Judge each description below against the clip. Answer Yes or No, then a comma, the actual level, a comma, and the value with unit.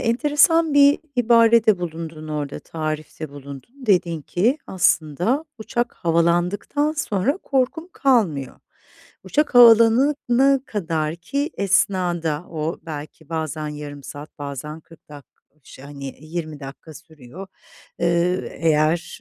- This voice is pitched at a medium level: Yes, medium, 170 Hz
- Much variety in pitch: Yes, wide, 7.3 semitones